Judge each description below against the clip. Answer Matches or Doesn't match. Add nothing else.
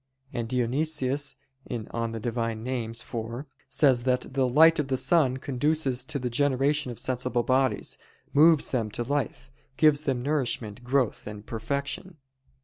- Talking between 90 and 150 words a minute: Matches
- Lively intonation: Doesn't match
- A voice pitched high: Doesn't match